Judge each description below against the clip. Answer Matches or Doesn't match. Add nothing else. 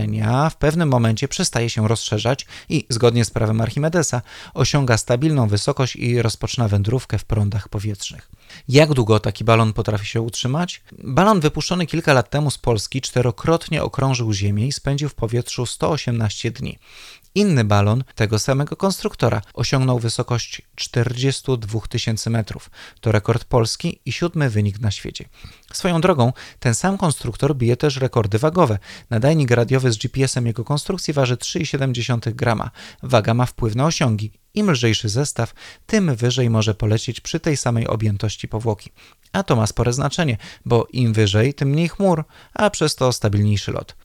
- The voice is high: Doesn't match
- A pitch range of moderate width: Matches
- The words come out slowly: Doesn't match